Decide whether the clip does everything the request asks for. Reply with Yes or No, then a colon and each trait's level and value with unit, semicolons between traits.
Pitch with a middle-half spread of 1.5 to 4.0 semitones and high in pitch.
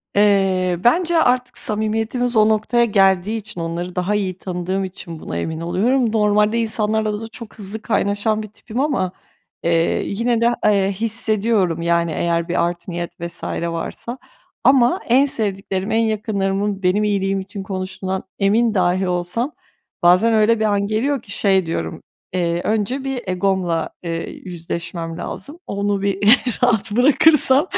Yes: average, 3.5 semitones; high, 200 Hz